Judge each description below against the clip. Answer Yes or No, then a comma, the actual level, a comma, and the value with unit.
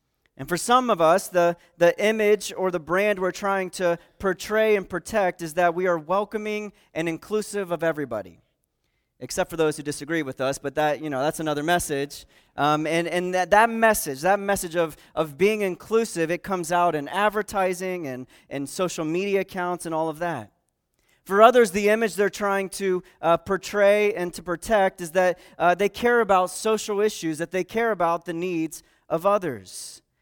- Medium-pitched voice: Yes, medium, 180 Hz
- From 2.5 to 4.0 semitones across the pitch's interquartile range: Yes, average, 3.6 semitones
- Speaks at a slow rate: No, average, 185 wpm